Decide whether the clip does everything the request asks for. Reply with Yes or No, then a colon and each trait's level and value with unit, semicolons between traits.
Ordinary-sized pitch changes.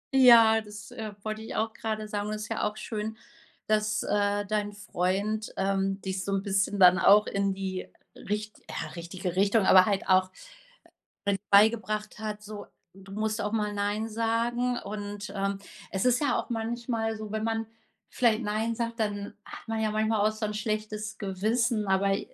No: narrow, 1.7 semitones